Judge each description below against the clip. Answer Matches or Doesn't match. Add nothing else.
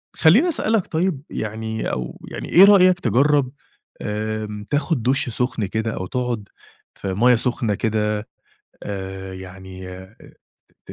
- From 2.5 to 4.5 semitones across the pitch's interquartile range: Doesn't match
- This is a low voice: Matches